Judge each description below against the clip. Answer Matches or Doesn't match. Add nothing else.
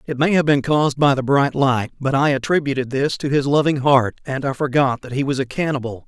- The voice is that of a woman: Doesn't match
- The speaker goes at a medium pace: Doesn't match